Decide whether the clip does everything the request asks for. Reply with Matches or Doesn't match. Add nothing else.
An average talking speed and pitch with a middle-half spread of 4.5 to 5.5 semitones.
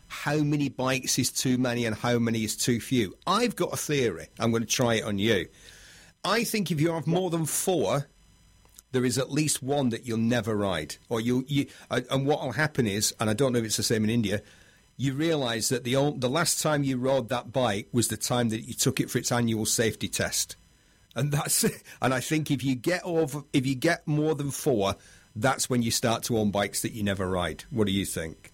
Doesn't match